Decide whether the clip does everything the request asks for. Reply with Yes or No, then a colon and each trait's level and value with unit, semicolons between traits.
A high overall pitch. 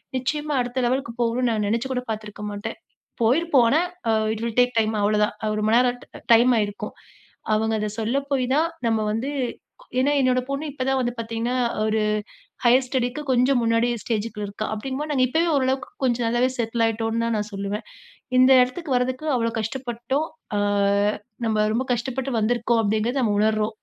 Yes: high, 240 Hz